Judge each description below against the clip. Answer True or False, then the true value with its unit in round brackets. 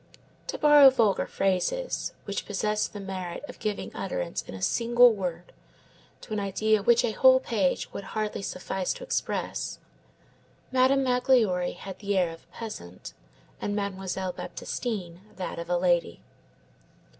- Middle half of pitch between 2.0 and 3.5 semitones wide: False (4.6 semitones)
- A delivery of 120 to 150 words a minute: True (145 wpm)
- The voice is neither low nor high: False (205 Hz)